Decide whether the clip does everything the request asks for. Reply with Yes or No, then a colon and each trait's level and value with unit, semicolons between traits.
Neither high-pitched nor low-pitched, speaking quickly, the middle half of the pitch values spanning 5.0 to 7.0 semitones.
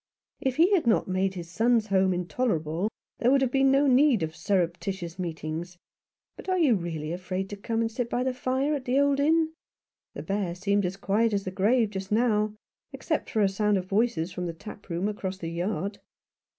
No: high, 205 Hz; fast, 215 wpm; average, 5.3 semitones